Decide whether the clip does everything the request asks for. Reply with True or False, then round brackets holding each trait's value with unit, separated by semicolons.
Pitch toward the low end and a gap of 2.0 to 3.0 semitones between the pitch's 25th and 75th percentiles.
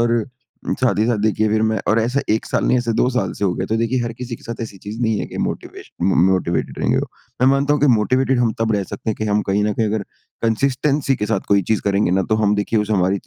True (110 Hz; 2.7 semitones)